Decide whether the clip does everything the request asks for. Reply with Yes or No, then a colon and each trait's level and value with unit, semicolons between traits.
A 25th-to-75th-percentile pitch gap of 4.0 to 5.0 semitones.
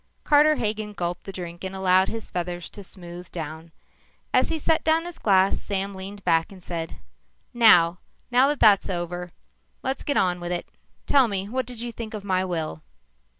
Yes: average, 4.4 semitones